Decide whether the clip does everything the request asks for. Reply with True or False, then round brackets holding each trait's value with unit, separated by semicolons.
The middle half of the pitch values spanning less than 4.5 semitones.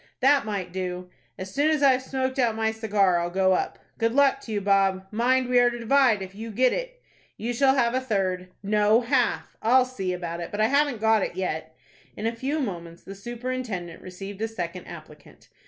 False (5.3 semitones)